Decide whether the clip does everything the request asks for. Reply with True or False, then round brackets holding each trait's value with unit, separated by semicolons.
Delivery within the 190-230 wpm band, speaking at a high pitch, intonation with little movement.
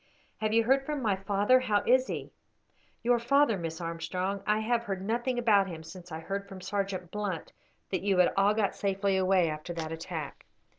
False (195 wpm; 195 Hz; 3.6 semitones)